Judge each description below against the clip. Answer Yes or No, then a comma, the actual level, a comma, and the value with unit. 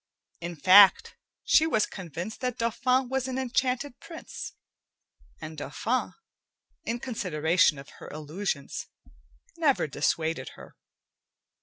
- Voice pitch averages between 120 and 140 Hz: No, high, 210 Hz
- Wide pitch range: Yes, wide, 8.0 semitones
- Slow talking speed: Yes, slow, 110 wpm